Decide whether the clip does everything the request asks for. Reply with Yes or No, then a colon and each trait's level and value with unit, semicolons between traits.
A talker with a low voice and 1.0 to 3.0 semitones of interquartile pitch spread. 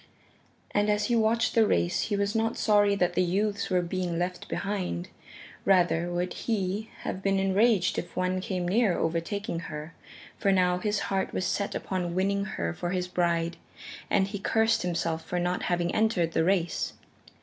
No: medium, 185 Hz; average, 2.7 semitones